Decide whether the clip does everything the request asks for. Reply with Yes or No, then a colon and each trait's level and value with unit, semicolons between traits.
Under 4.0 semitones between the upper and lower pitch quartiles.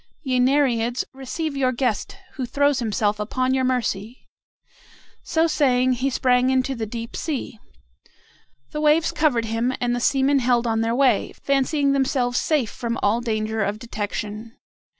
Yes: average, 3.1 semitones